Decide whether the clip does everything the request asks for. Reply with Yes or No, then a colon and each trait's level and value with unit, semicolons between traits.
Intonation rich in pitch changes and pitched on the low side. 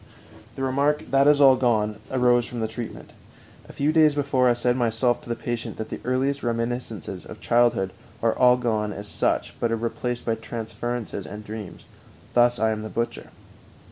No: narrow, 2.4 semitones; low, 120 Hz